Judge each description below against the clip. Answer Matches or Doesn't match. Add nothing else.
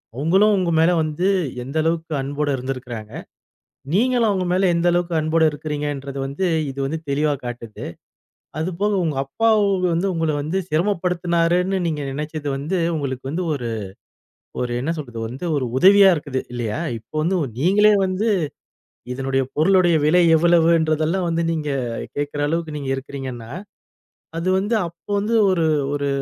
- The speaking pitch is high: Doesn't match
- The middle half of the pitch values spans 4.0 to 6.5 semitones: Matches